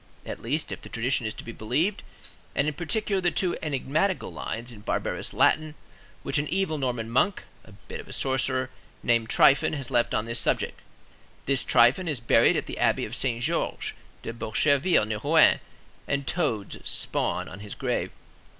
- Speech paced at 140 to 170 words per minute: No, average, 180 wpm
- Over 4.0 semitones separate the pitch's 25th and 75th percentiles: Yes, average, 5.0 semitones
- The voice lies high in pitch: No, low, 130 Hz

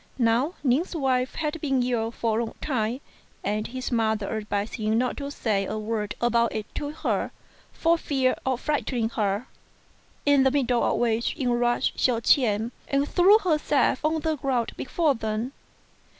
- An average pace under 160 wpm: No, average, 175 wpm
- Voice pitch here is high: Yes, high, 245 Hz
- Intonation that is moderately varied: Yes, average, 4.2 semitones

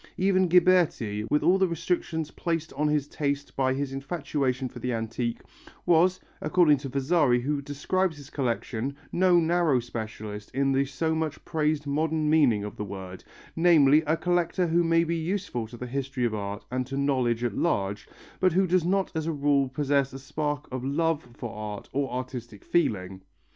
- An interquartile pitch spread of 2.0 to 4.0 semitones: No, average, 4.9 semitones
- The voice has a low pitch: No, medium, 145 Hz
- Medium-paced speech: Yes, average, 180 wpm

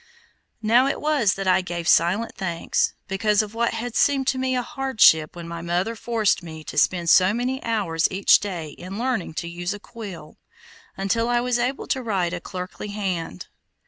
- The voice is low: No, high, 200 Hz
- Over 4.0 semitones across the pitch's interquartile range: Yes, average, 5.3 semitones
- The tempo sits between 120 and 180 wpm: No, average, 190 wpm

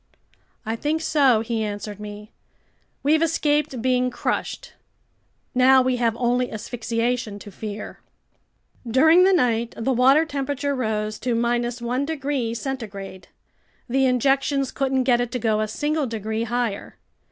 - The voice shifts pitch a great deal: No, average, 3.3 semitones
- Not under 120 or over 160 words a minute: Yes, slow, 135 wpm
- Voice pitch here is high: Yes, high, 245 Hz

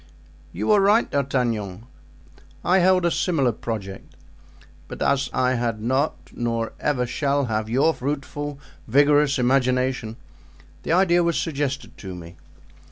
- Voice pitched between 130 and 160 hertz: Yes, low, 135 Hz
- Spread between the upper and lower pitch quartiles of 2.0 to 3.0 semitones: No, average, 4.1 semitones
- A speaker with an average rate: No, slow, 130 wpm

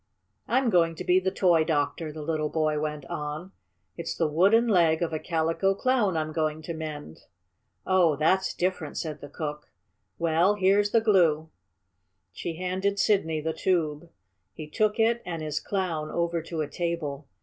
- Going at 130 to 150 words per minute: No, average, 170 wpm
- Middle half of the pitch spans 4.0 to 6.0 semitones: No, average, 3.4 semitones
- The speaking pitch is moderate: Yes, medium, 165 Hz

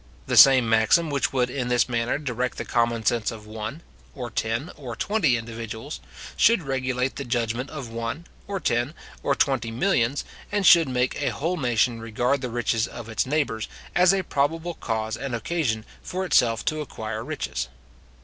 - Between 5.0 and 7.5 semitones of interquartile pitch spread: No, average, 4.2 semitones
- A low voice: Yes, low, 125 Hz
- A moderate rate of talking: Yes, average, 175 wpm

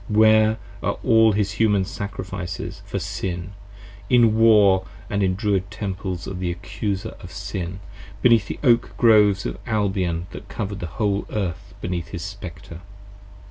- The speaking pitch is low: Yes, low, 100 Hz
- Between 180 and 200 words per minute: No, average, 155 wpm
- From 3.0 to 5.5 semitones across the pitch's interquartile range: No, narrow, 2.6 semitones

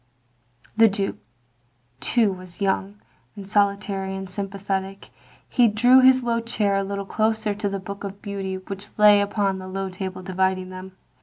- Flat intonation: Yes, narrow, 1.6 semitones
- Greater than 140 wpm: Yes, average, 165 wpm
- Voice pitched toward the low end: No, high, 200 Hz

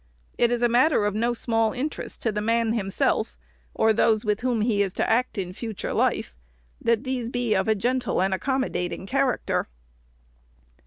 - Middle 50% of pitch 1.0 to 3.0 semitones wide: Yes, average, 2.7 semitones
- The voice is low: No, high, 230 Hz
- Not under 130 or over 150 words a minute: No, average, 175 wpm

